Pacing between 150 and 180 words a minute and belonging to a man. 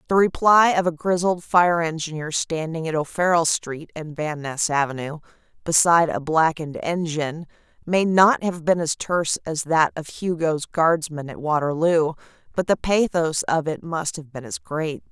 No: average, 165 wpm; female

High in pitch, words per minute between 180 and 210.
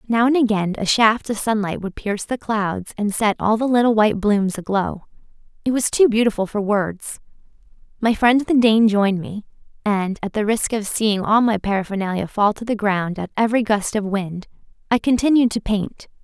Yes: high, 215 Hz; average, 190 wpm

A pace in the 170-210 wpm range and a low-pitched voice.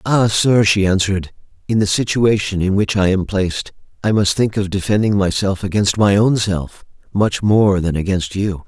Yes: average, 185 wpm; low, 100 Hz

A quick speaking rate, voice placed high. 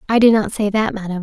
Yes: fast, 295 wpm; high, 210 Hz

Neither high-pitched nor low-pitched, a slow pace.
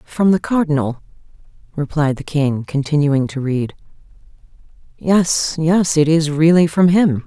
Yes: medium, 155 Hz; slow, 130 wpm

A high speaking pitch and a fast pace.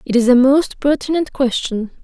No: very high, 265 Hz; average, 175 wpm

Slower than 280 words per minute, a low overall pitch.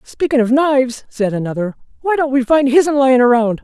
No: average, 200 wpm; very high, 260 Hz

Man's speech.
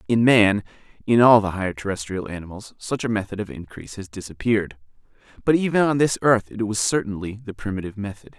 Yes: male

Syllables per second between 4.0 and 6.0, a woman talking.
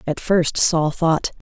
No: 3.3 syllables/s; female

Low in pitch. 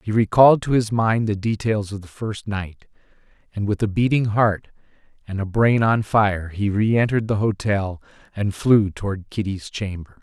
Yes: low, 105 Hz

